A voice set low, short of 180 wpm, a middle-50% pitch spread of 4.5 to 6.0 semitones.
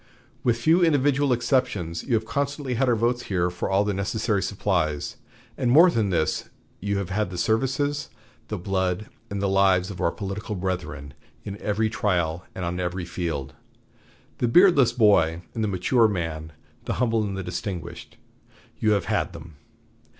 Yes: low, 100 Hz; average, 170 wpm; average, 5.0 semitones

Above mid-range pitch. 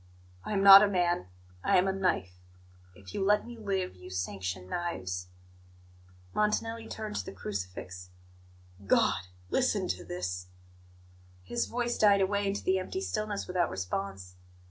No: medium, 175 Hz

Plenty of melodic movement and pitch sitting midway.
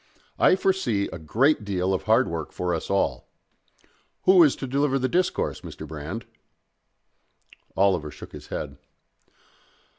No: wide, 7.6 semitones; low, 100 Hz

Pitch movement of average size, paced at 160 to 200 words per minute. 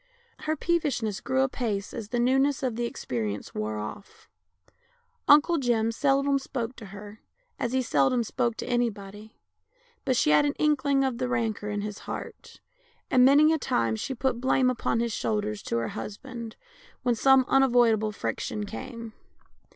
Yes: average, 4.0 semitones; average, 165 wpm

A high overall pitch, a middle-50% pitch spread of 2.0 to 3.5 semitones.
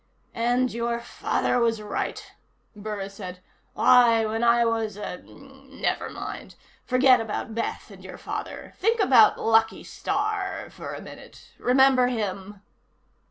Yes: high, 235 Hz; average, 2.9 semitones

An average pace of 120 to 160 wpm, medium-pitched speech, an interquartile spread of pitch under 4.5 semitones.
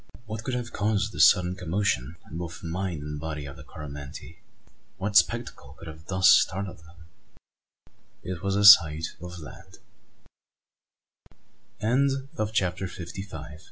No: average, 140 wpm; very low, 90 Hz; average, 4.0 semitones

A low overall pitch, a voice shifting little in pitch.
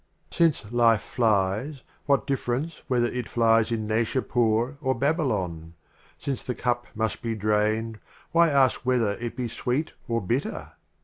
No: low, 120 Hz; average, 3.2 semitones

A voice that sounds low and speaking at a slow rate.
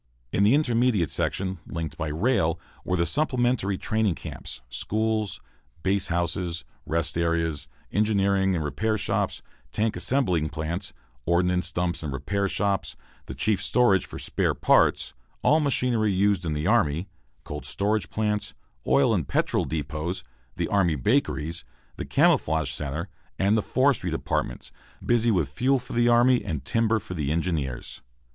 No: very low, 95 Hz; average, 145 wpm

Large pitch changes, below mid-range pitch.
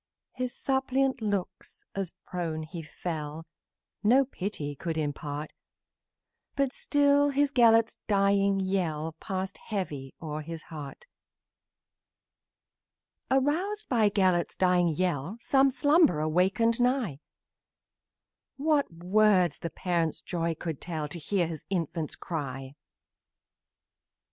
No: wide, 7.3 semitones; medium, 185 Hz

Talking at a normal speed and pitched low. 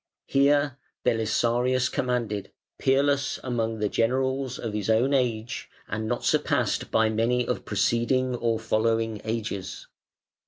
No: slow, 120 wpm; low, 115 Hz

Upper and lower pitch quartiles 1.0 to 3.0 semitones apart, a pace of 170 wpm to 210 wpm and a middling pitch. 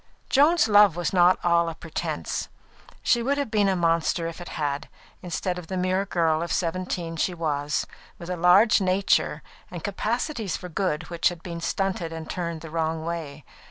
Yes: narrow, 2.6 semitones; average, 190 wpm; medium, 175 Hz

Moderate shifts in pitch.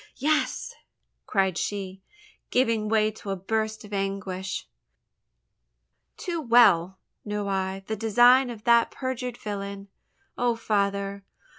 Yes: average, 3.1 semitones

